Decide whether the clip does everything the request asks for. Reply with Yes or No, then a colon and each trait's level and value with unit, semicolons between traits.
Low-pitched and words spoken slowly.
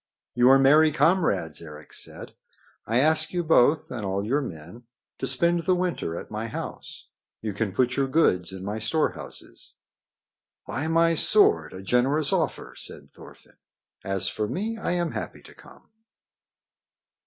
No: low, 130 Hz; average, 155 wpm